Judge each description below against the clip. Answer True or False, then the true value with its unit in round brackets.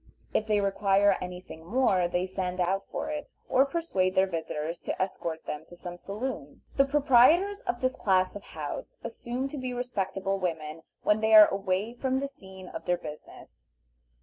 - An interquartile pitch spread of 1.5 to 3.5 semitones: False (5.6 semitones)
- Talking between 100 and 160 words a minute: False (180 wpm)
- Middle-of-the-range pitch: False (195 Hz)